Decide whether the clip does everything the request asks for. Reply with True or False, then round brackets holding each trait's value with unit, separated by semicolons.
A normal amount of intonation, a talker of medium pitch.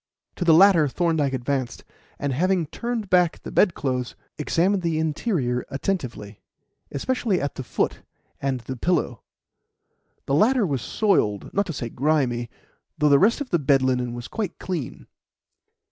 False (6.3 semitones; 150 Hz)